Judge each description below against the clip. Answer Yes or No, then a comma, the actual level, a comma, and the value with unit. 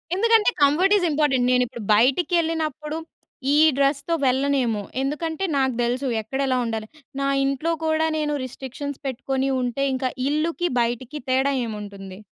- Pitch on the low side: No, very high, 275 Hz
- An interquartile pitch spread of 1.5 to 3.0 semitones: No, average, 3.6 semitones